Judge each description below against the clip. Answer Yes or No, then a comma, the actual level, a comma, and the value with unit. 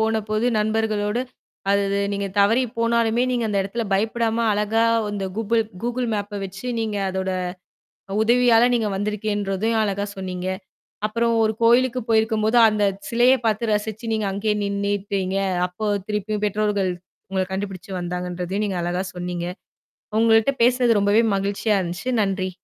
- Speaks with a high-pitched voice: Yes, high, 210 Hz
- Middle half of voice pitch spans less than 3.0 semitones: Yes, narrow, 2.4 semitones